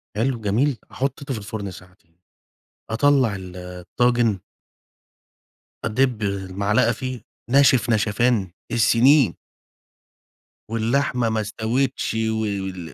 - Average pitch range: Yes, average, 3.9 semitones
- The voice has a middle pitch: No, low, 110 Hz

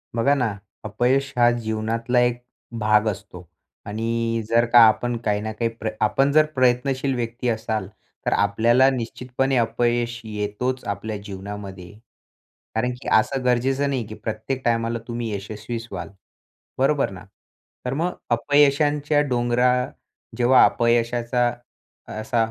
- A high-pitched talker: No, low, 120 Hz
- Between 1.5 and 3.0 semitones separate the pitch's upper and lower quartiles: Yes, narrow, 2.5 semitones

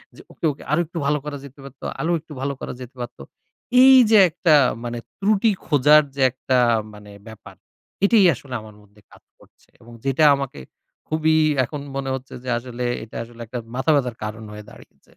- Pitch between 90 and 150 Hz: Yes, low, 135 Hz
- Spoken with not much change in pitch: No, average, 4.4 semitones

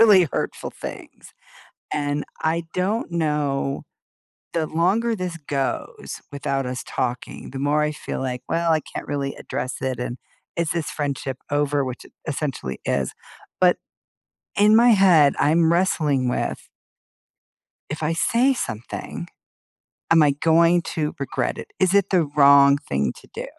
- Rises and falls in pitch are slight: No, average, 3.6 semitones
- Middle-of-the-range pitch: Yes, medium, 150 Hz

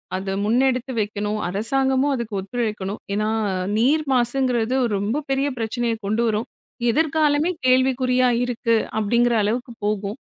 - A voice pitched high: Yes, high, 240 Hz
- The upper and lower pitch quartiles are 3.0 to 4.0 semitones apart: Yes, average, 3.6 semitones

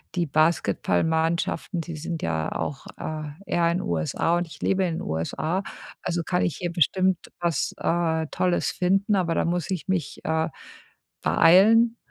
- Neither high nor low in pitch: Yes, medium, 170 Hz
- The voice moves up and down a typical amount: No, narrow, 2.2 semitones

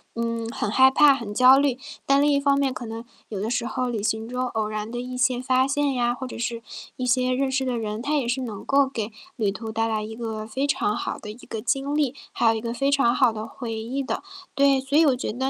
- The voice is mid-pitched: No, high, 245 Hz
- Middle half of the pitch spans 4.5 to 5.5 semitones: No, average, 3.1 semitones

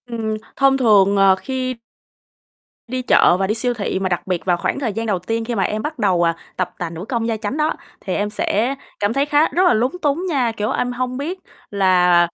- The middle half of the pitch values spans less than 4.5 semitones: No, average, 5.0 semitones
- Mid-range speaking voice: No, high, 225 Hz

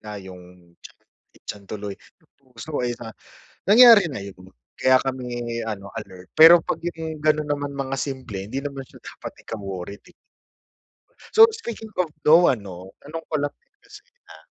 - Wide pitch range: Yes, wide, 7.6 semitones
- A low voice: Yes, low, 130 Hz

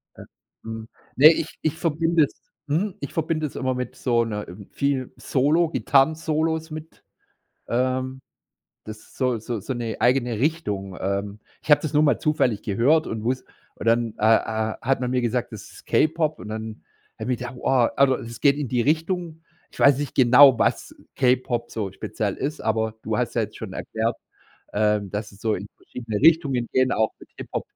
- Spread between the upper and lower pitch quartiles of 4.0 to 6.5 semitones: Yes, average, 5.1 semitones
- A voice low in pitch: Yes, low, 125 Hz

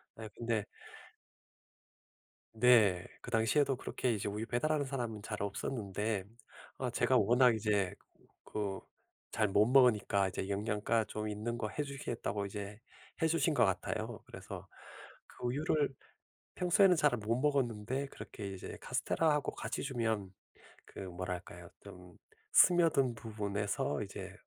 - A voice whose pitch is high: No, low, 110 Hz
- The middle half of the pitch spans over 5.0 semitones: No, average, 4.3 semitones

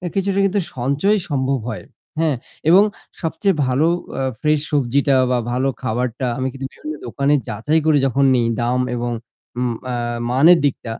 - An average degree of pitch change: Yes, average, 4.0 semitones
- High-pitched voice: No, low, 135 Hz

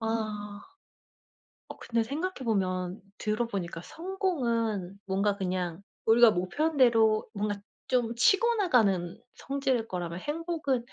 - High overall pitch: Yes, high, 225 Hz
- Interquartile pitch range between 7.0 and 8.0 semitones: No, wide, 5.4 semitones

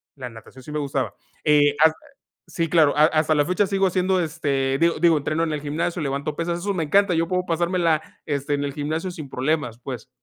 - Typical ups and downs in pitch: Yes, average, 3.1 semitones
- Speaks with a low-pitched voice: No, medium, 155 Hz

